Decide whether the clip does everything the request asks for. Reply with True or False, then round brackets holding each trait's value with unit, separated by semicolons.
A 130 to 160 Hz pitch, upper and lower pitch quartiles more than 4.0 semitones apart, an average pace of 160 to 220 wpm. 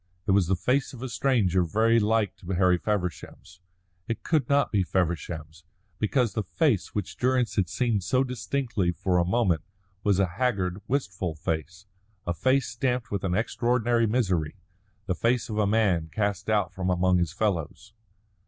False (100 Hz; 4.8 semitones; 170 wpm)